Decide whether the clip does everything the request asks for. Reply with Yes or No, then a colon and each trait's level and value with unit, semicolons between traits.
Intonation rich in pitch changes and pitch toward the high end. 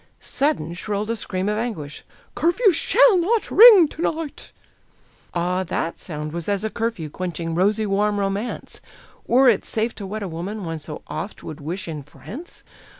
Yes: wide, 6.0 semitones; high, 205 Hz